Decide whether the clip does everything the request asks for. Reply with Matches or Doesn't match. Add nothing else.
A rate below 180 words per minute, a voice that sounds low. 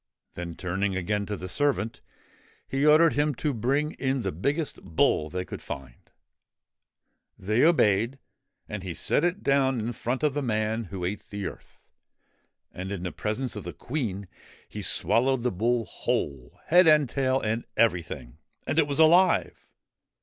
Matches